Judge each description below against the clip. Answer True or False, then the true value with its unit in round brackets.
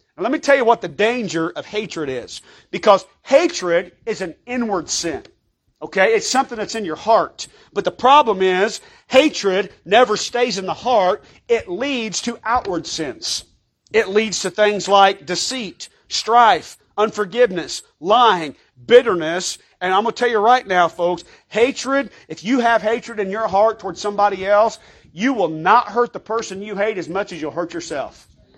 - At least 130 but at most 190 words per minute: True (170 wpm)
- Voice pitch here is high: True (210 Hz)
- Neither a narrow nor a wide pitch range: True (4.3 semitones)